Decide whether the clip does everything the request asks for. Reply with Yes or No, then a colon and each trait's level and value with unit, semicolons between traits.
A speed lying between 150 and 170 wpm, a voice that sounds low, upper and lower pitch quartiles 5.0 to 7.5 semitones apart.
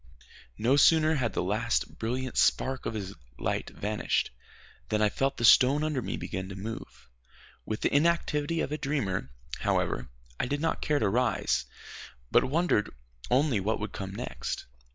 Yes: average, 165 wpm; low, 125 Hz; wide, 5.5 semitones